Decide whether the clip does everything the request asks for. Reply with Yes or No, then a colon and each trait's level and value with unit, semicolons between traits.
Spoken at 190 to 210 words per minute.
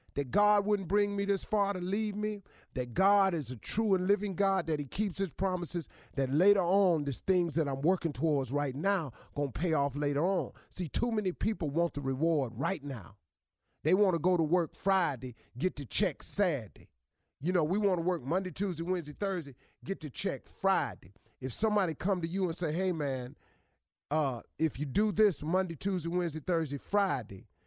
Yes: average, 200 wpm